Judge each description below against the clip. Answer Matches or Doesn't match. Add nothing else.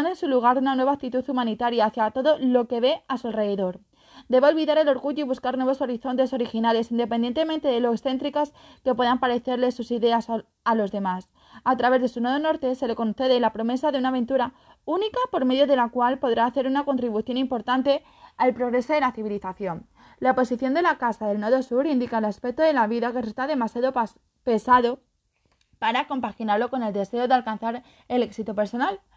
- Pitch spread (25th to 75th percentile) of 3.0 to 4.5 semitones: Doesn't match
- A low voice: Doesn't match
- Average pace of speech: Doesn't match